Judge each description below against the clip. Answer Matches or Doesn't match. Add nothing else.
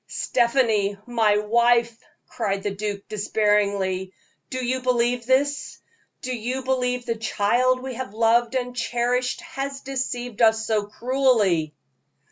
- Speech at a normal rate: Doesn't match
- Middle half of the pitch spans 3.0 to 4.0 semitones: Matches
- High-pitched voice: Matches